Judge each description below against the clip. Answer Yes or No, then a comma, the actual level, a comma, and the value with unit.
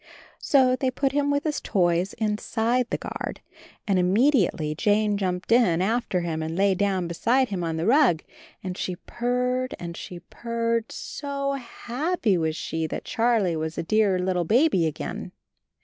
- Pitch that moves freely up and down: Yes, wide, 6.1 semitones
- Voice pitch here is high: Yes, high, 210 Hz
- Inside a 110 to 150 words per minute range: No, average, 165 wpm